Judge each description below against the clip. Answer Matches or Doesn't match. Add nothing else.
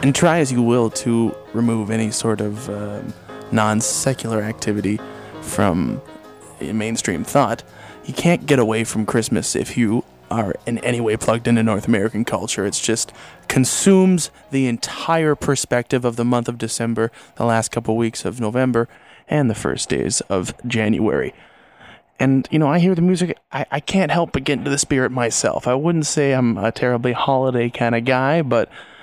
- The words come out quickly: Doesn't match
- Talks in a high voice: Doesn't match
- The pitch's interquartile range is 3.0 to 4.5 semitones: Matches